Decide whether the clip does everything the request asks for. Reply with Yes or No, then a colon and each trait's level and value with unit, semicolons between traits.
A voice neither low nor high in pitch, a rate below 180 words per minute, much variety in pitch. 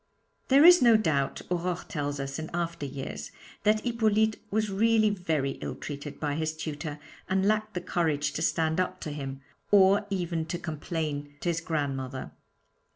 Yes: medium, 165 Hz; average, 165 wpm; wide, 5.7 semitones